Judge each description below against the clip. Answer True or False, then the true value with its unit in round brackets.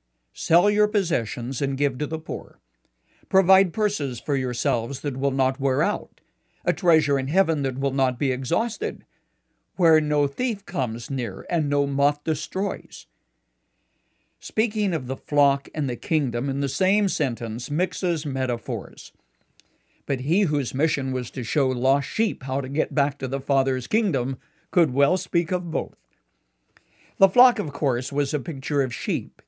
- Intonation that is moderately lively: True (4.8 semitones)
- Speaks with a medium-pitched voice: True (145 Hz)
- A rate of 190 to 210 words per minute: False (160 wpm)